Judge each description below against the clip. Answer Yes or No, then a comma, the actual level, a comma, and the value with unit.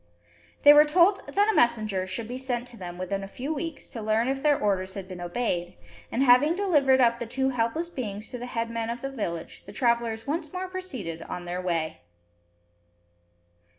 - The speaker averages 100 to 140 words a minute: No, average, 195 wpm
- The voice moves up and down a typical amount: No, wide, 5.9 semitones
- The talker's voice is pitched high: Yes, high, 235 Hz